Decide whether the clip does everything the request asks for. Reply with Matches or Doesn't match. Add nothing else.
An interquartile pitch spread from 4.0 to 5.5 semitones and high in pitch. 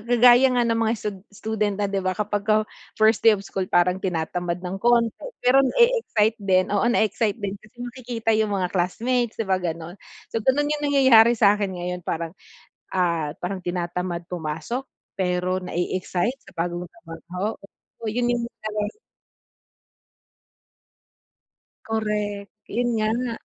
Matches